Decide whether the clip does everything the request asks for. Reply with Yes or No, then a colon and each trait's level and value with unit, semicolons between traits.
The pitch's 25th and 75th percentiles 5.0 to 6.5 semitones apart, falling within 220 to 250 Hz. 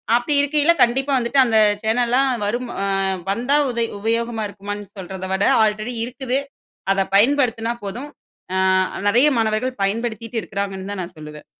No: average, 3.5 semitones; high, 230 Hz